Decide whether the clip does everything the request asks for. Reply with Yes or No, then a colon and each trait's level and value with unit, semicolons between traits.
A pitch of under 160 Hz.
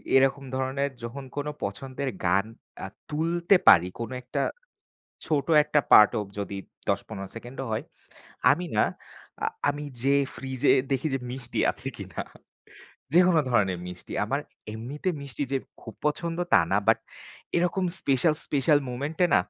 Yes: low, 135 Hz